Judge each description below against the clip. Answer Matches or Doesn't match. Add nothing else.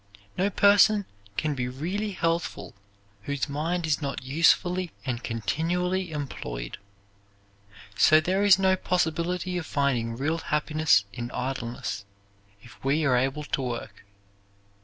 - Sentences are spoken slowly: Matches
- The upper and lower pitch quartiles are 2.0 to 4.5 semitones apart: Doesn't match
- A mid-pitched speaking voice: Matches